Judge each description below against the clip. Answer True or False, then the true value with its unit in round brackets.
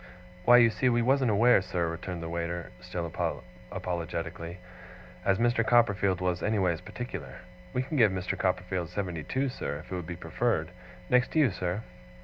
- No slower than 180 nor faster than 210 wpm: False (165 wpm)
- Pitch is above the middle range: False (95 Hz)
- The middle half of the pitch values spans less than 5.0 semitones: False (5.3 semitones)